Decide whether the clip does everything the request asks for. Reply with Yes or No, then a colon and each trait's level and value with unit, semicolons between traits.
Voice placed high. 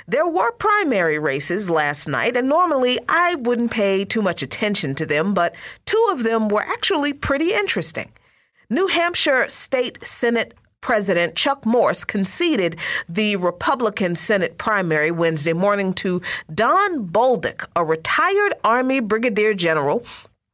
Yes: high, 215 Hz